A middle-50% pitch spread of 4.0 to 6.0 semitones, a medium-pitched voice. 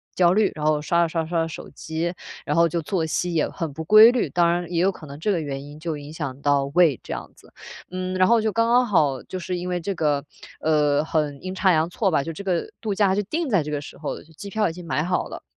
No: average, 3.5 semitones; medium, 170 Hz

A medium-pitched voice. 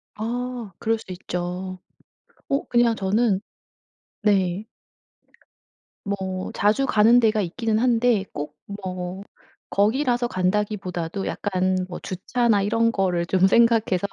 No: high, 205 Hz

